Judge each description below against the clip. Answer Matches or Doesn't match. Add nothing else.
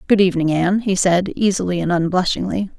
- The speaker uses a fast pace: Doesn't match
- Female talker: Matches